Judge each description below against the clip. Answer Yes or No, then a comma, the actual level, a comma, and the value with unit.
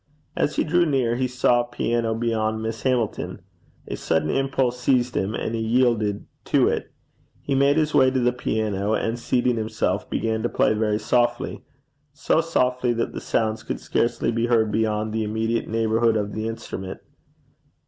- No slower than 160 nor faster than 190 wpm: Yes, average, 175 wpm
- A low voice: Yes, low, 115 Hz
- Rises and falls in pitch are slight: Yes, narrow, 2.2 semitones